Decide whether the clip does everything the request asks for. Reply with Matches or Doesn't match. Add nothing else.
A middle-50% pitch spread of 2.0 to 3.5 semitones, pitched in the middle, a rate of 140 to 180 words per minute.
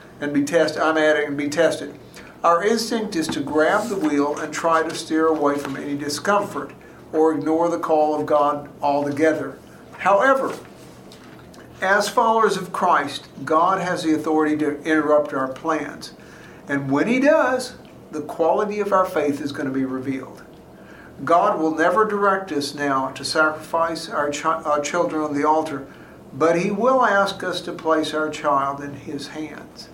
Matches